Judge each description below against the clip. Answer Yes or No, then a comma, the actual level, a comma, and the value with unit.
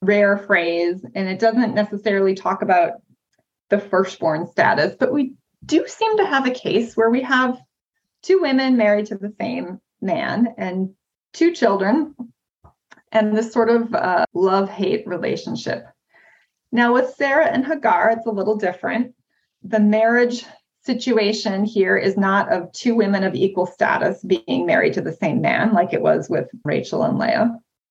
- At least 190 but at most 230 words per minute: No, average, 160 wpm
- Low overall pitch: No, high, 220 Hz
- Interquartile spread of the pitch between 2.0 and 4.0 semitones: Yes, average, 3.7 semitones